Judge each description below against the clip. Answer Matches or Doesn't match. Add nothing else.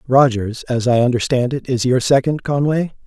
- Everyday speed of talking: Matches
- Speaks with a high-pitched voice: Doesn't match